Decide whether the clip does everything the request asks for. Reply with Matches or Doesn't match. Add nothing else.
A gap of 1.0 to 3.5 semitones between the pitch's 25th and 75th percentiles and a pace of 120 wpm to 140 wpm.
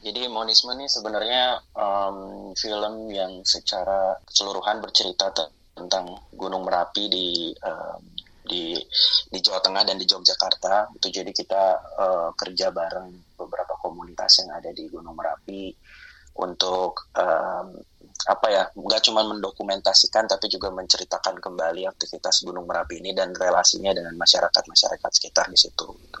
Matches